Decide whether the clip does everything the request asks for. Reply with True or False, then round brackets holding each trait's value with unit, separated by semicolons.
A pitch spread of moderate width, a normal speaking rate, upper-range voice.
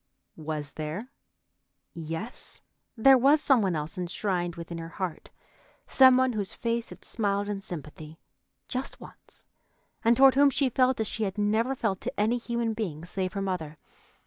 False (5.7 semitones; 165 wpm; 205 Hz)